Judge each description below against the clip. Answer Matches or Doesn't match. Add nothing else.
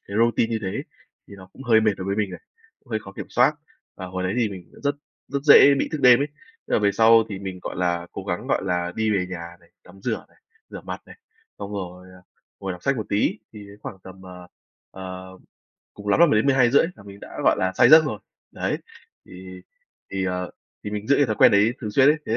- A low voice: Matches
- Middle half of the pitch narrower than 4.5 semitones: Matches